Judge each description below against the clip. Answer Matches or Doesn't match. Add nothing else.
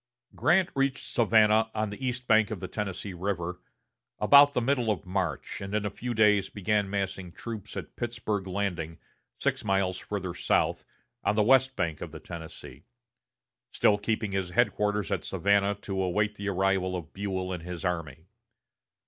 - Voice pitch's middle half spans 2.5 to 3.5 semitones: Matches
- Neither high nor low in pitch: Doesn't match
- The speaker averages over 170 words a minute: Doesn't match